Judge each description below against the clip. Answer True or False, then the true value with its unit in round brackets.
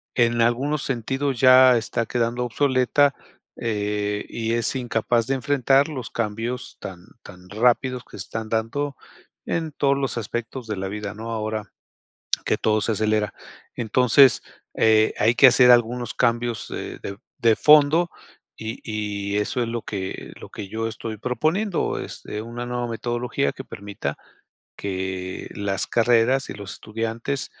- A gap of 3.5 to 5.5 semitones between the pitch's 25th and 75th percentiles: False (3.0 semitones)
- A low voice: True (115 Hz)